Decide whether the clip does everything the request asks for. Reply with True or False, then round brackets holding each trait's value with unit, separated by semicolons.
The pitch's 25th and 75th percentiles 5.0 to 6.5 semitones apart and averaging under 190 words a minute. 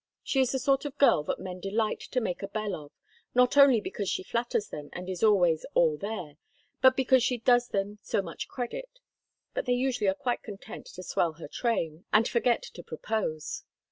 False (5.4 semitones; 205 wpm)